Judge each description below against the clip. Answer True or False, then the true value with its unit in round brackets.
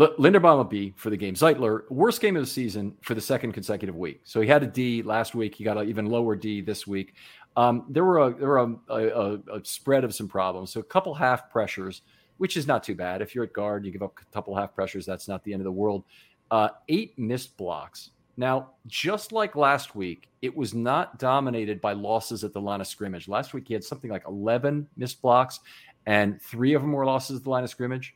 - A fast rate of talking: True (245 wpm)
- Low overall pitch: True (115 Hz)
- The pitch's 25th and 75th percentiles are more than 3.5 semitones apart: True (4.2 semitones)